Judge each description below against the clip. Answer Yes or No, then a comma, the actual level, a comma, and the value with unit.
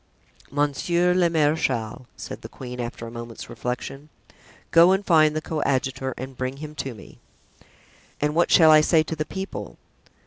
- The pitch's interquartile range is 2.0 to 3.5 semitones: No, average, 3.9 semitones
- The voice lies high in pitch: No, medium, 145 Hz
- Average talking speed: Yes, average, 165 wpm